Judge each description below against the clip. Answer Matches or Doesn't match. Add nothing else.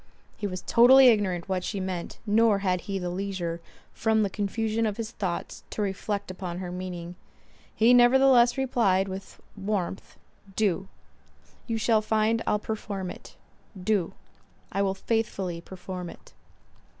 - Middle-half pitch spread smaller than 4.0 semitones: Matches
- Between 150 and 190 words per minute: Doesn't match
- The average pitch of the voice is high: Matches